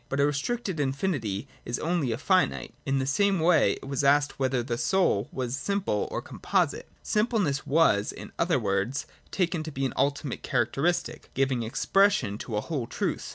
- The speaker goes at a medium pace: Yes, average, 180 wpm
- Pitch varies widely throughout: Yes, wide, 5.9 semitones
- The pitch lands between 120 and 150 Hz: Yes, medium, 140 Hz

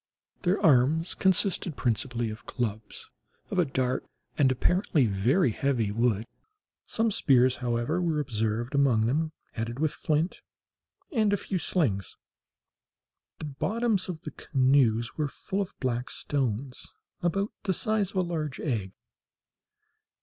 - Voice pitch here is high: No, medium, 140 Hz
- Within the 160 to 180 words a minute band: No, slow, 135 wpm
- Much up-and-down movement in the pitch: Yes, wide, 6.7 semitones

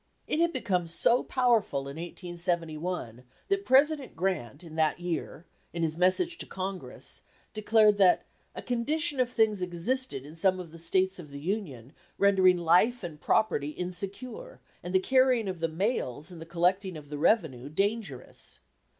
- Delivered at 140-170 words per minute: Yes, average, 160 wpm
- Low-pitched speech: No, medium, 185 Hz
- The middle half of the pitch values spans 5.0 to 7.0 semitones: Yes, wide, 5.5 semitones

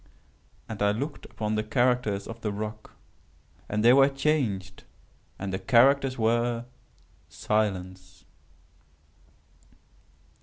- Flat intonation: No, average, 3.4 semitones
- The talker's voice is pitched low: Yes, low, 110 Hz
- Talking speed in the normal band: No, slow, 105 wpm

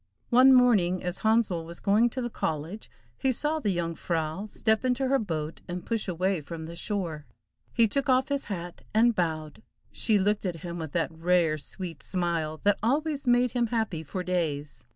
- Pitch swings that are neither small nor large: No, wide, 6.0 semitones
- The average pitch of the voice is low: No, medium, 185 Hz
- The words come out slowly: No, average, 190 wpm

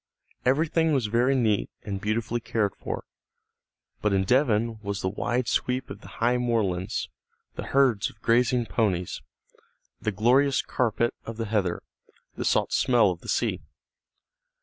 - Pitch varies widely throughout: No, average, 3.3 semitones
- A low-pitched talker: Yes, low, 115 Hz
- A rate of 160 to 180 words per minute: No, average, 150 wpm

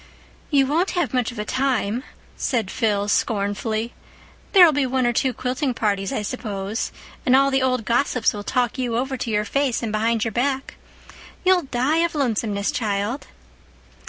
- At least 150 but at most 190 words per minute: Yes, average, 170 wpm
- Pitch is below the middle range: No, high, 245 Hz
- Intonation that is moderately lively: Yes, average, 3.8 semitones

